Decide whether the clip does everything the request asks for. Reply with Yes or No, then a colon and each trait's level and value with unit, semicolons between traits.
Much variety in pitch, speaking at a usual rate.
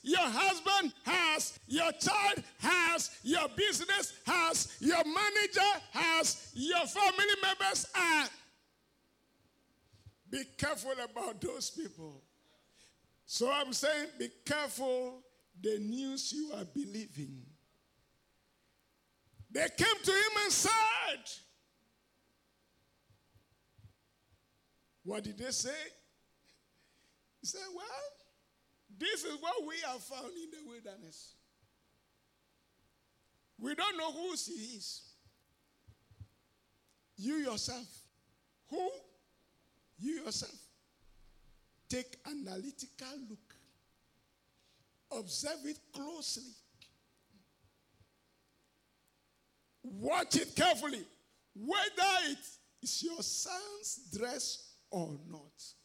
No: wide, 8.1 semitones; slow, 85 wpm